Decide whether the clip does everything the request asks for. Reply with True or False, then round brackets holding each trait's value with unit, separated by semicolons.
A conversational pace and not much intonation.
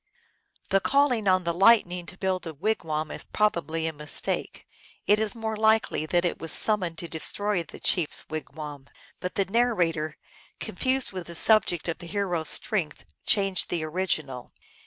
False (180 wpm; 4.7 semitones)